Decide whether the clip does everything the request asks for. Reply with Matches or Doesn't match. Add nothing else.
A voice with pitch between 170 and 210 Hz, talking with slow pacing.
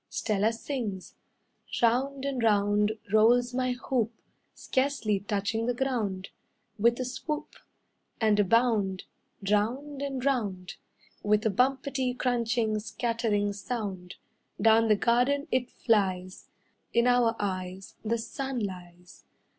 Doesn't match